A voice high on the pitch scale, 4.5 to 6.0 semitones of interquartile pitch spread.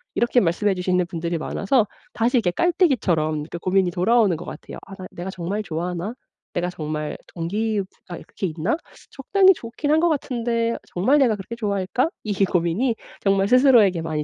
Yes: high, 195 Hz; average, 5.3 semitones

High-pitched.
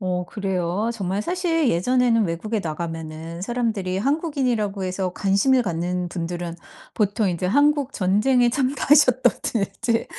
Yes: high, 205 Hz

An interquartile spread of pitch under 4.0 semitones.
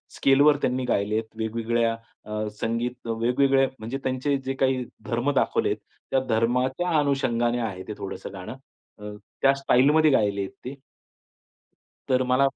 Yes: average, 3.2 semitones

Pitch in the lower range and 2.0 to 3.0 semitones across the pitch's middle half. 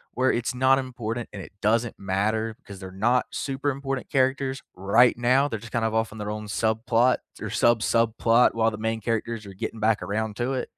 Yes: low, 115 Hz; average, 2.7 semitones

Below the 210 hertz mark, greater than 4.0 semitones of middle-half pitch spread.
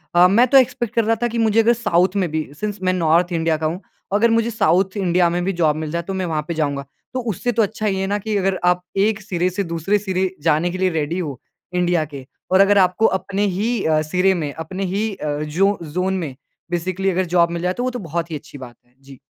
No: medium, 185 Hz; average, 3.7 semitones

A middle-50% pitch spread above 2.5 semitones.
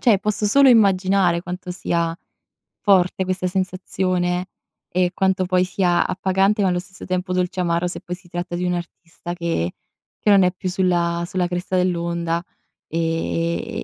No: narrow, 1.3 semitones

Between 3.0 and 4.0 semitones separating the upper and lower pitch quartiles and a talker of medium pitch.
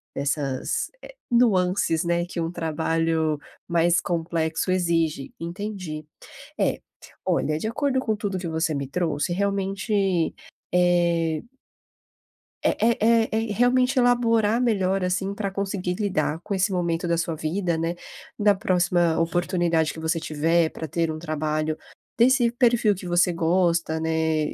Yes: average, 3.7 semitones; medium, 175 Hz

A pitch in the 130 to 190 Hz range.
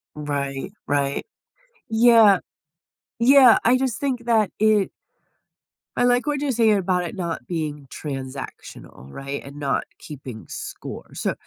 Yes: medium, 185 Hz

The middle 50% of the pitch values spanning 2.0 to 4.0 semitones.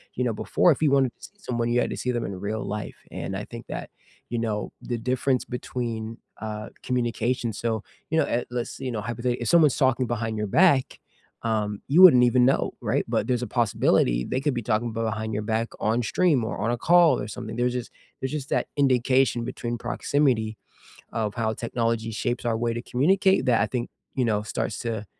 Yes: narrow, 2.5 semitones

